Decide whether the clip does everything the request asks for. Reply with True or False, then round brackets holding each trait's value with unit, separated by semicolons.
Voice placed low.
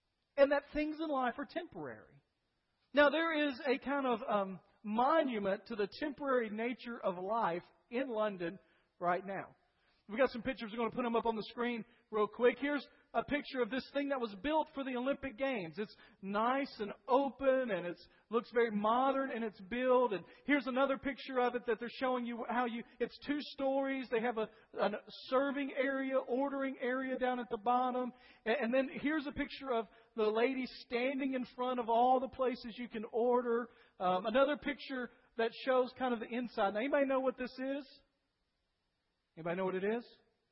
False (245 Hz)